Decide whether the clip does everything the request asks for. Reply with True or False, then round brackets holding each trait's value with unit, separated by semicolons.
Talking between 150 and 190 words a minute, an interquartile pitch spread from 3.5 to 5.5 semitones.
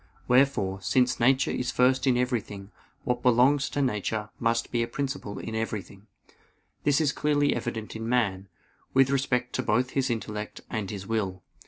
True (165 wpm; 3.8 semitones)